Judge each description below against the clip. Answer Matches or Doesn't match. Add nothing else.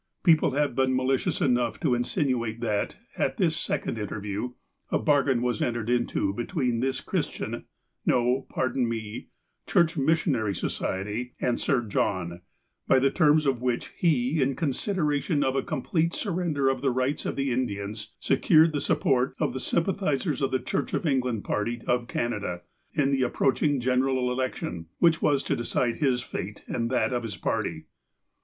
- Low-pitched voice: Matches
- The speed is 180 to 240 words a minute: Doesn't match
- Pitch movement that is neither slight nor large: Matches